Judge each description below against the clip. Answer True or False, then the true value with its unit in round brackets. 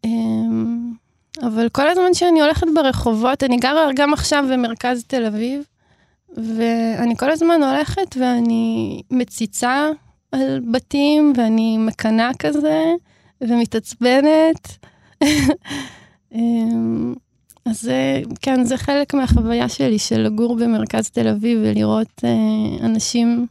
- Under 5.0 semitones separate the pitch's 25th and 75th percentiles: True (4.1 semitones)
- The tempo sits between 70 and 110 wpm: True (105 wpm)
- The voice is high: True (235 Hz)